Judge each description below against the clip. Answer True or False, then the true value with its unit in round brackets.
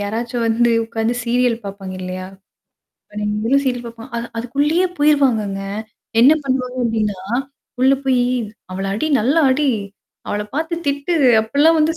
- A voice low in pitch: False (240 Hz)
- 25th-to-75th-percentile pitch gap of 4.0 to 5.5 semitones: True (4.4 semitones)